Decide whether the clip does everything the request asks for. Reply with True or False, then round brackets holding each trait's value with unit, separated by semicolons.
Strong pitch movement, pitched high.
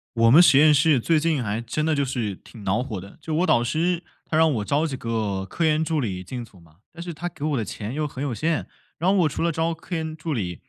False (6.1 semitones; 145 Hz)